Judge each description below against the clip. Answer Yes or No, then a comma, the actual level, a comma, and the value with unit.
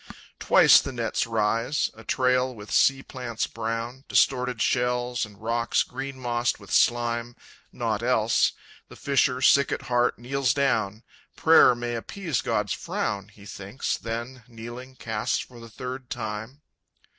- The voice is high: No, low, 120 Hz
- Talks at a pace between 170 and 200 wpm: No, average, 145 wpm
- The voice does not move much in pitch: Yes, narrow, 2.2 semitones